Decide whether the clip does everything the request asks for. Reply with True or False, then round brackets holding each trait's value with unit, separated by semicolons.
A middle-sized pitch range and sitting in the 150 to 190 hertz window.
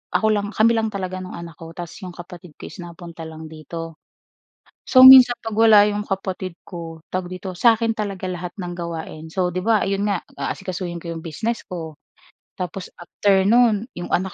True (3.4 semitones; 185 Hz)